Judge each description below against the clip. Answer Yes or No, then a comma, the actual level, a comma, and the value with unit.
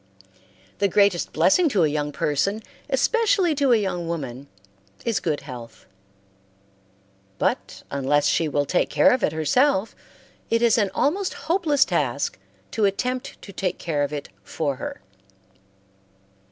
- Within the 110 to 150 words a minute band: Yes, average, 140 wpm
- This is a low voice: No, high, 190 Hz